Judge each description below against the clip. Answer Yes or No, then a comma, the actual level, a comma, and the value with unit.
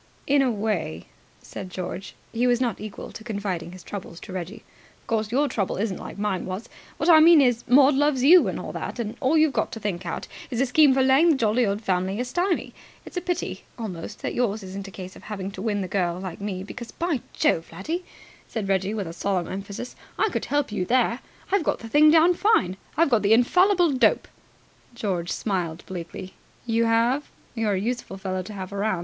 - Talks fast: Yes, fast, 215 wpm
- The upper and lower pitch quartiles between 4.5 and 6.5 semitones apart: Yes, wide, 5.5 semitones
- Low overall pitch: No, high, 220 Hz